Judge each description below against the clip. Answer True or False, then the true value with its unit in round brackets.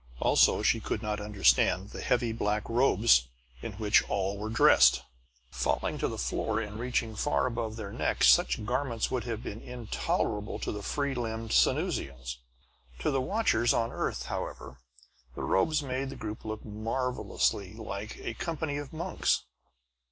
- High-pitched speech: False (110 Hz)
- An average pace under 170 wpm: True (160 wpm)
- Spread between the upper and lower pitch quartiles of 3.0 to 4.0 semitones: True (3.4 semitones)